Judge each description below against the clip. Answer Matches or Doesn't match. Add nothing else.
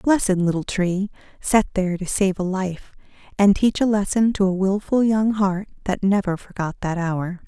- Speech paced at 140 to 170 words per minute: Doesn't match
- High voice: Matches